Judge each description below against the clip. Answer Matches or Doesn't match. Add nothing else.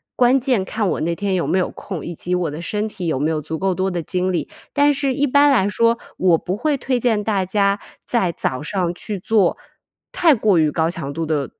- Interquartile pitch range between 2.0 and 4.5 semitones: Doesn't match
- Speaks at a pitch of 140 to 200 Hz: Matches